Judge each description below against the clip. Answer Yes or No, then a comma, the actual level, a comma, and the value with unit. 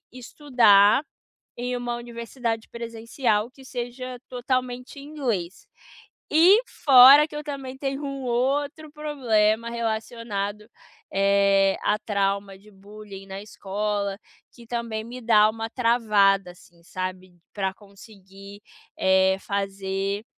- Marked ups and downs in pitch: No, average, 4.1 semitones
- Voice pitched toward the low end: No, high, 225 Hz